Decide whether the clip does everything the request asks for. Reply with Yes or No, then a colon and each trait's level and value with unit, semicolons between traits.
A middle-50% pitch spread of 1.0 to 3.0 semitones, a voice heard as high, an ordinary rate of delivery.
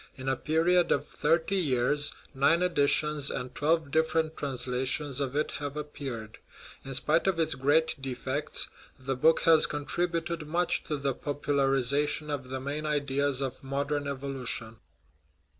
No: average, 2.7 semitones; medium, 145 Hz; average, 145 wpm